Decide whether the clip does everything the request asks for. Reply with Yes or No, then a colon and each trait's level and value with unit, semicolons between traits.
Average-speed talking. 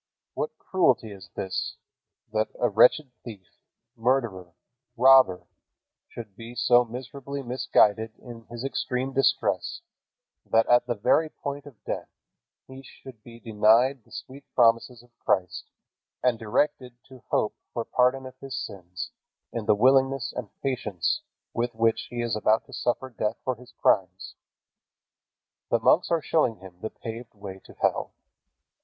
Yes: average, 145 wpm